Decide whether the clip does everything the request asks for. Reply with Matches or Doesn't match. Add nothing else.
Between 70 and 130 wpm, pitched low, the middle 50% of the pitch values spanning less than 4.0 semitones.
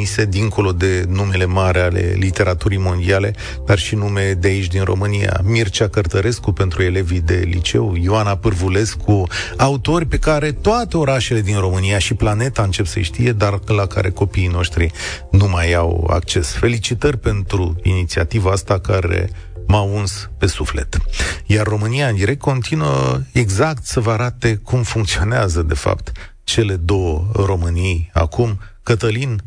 Doesn't match